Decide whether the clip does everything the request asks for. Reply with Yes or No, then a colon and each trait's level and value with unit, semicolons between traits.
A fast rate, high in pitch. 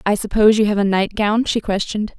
Yes: fast, 220 wpm; high, 210 Hz